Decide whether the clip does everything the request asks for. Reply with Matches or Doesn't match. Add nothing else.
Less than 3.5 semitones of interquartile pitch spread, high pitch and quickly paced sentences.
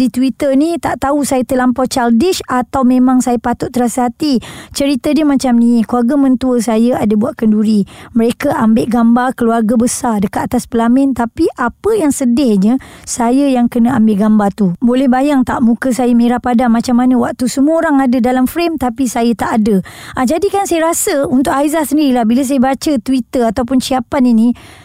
Matches